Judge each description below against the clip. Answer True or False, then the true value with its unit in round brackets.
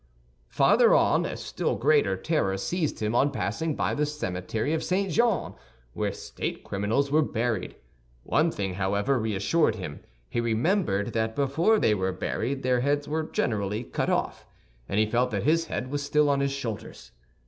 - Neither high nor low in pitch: False (125 Hz)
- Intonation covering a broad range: True (6.2 semitones)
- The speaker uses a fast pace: False (170 wpm)